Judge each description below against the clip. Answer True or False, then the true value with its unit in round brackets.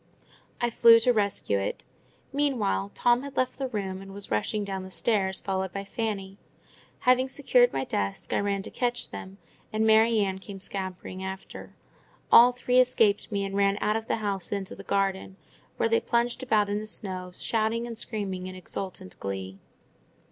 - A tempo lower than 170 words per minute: False (180 wpm)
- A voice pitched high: True (200 Hz)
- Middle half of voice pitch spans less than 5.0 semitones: True (3.4 semitones)